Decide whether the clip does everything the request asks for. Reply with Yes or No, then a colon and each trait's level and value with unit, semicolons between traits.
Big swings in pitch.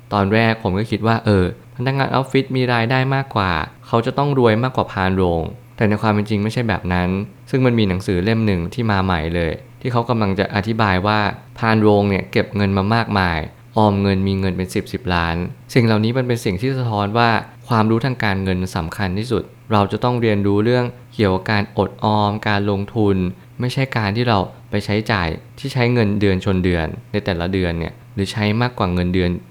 No: average, 3.8 semitones